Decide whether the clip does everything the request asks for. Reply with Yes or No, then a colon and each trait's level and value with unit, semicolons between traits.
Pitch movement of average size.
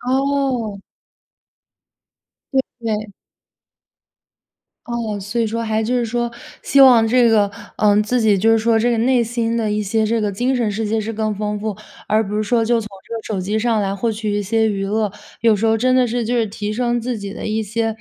No: narrow, 2.0 semitones